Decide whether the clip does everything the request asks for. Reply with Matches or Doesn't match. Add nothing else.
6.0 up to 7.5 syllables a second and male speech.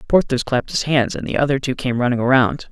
Matches